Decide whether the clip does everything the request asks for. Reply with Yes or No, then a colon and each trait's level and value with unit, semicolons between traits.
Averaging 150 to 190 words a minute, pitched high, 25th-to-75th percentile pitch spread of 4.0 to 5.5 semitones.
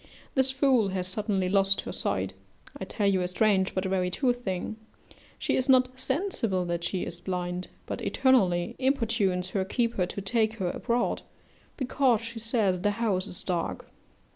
Yes: average, 170 wpm; high, 200 Hz; average, 4.7 semitones